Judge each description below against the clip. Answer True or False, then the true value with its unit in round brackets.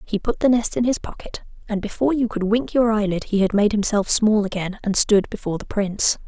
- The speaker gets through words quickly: True (240 wpm)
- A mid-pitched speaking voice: False (210 Hz)